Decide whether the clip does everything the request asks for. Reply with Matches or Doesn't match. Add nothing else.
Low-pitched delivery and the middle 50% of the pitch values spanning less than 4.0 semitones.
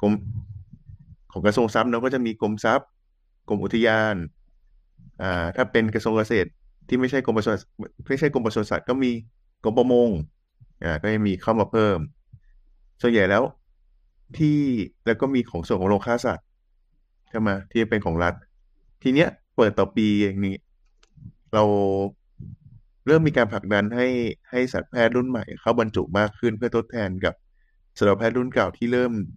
Matches